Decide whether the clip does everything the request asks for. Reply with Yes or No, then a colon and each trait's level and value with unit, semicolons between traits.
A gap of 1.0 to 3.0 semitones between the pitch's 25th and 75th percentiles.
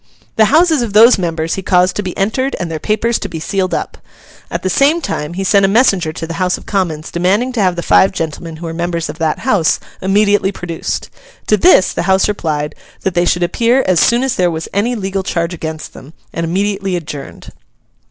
No: average, 4.0 semitones